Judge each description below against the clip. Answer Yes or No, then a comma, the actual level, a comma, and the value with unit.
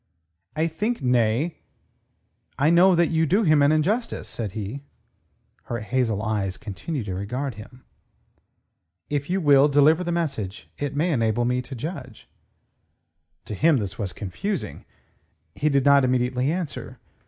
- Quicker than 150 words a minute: No, average, 145 wpm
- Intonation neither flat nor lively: No, wide, 6.0 semitones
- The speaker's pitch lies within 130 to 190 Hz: Yes, medium, 140 Hz